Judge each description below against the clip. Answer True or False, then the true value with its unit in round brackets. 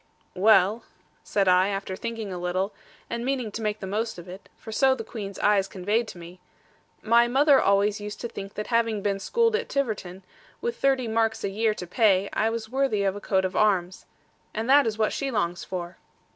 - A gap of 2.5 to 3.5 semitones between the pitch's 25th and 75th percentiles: True (3.2 semitones)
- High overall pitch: True (210 Hz)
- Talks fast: True (210 wpm)